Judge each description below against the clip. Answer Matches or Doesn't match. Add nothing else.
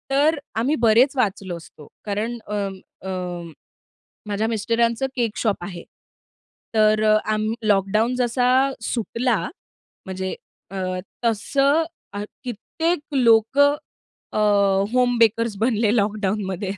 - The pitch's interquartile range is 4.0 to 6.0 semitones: Doesn't match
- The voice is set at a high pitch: Matches